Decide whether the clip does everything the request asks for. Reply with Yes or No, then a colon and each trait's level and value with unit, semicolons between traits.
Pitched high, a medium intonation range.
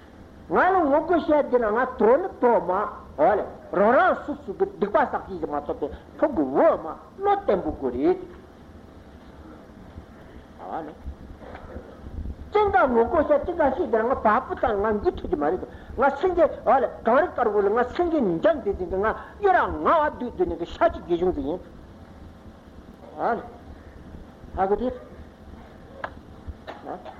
No: very high, 285 Hz; wide, 8.0 semitones